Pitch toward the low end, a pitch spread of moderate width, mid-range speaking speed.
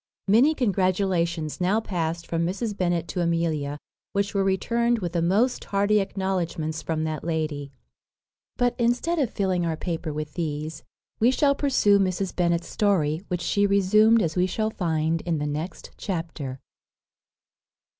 No: medium, 180 Hz; average, 3.9 semitones; average, 150 wpm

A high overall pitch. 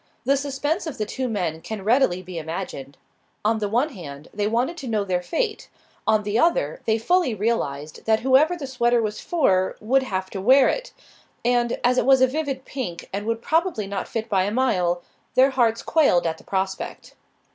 Yes: high, 225 Hz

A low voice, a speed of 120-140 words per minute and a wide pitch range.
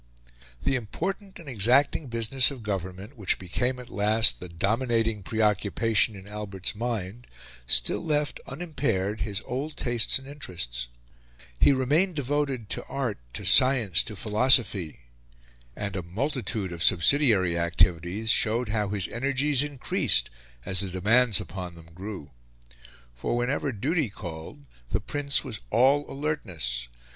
Yes: low, 110 Hz; slow, 135 wpm; wide, 6.0 semitones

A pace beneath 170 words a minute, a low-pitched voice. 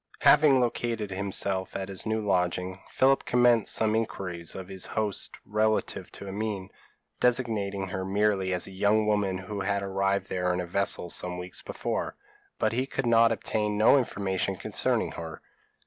Yes: average, 160 wpm; low, 100 Hz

